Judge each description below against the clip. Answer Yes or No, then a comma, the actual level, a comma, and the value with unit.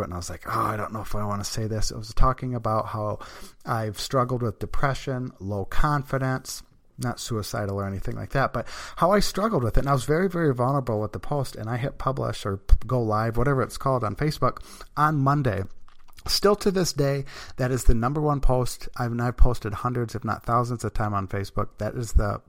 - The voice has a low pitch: Yes, low, 120 Hz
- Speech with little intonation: No, average, 4.2 semitones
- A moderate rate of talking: No, fast, 225 wpm